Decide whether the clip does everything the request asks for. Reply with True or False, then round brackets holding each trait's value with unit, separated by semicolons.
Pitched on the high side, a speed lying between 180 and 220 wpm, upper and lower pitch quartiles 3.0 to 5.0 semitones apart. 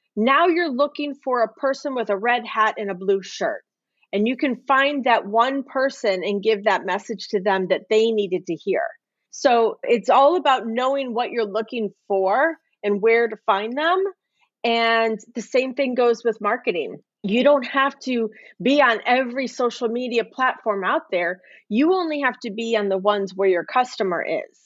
True (235 Hz; 185 wpm; 4.1 semitones)